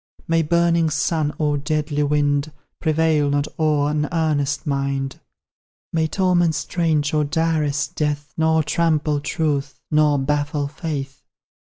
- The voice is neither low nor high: Yes, medium, 150 Hz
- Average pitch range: No, narrow, 1.8 semitones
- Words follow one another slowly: Yes, slow, 125 wpm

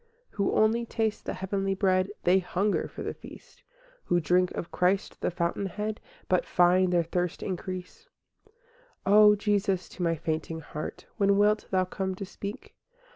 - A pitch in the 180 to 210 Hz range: Yes, high, 190 Hz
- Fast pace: No, average, 165 wpm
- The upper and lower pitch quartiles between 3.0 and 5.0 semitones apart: No, narrow, 2.4 semitones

